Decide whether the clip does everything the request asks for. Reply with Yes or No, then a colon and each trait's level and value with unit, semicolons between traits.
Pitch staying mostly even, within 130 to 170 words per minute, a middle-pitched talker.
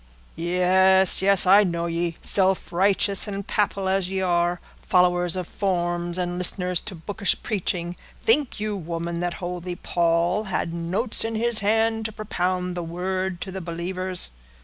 Yes: narrow, 2.2 semitones; average, 150 wpm; medium, 180 Hz